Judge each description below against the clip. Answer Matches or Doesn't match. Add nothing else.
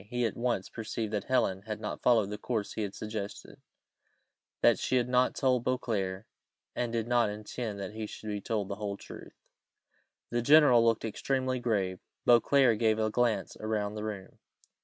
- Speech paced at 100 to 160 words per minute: Doesn't match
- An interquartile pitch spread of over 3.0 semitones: Doesn't match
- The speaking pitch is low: Matches